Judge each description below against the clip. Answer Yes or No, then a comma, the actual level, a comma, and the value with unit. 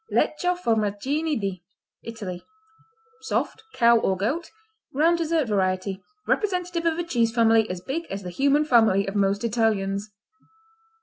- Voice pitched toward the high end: Yes, high, 230 Hz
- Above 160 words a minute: No, slow, 135 wpm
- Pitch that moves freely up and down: Yes, wide, 7.8 semitones